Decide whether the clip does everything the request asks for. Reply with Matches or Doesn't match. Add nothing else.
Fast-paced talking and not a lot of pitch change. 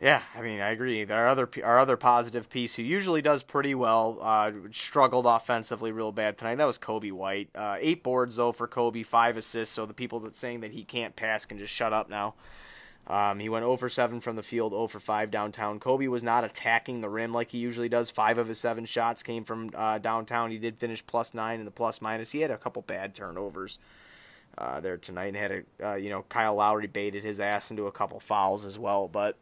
Matches